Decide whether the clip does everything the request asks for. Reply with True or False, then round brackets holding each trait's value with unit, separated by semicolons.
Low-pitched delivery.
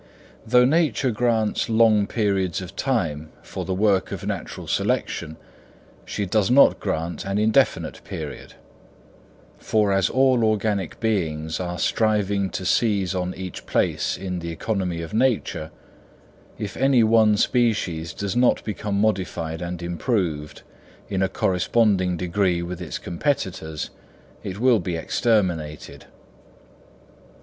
True (100 Hz)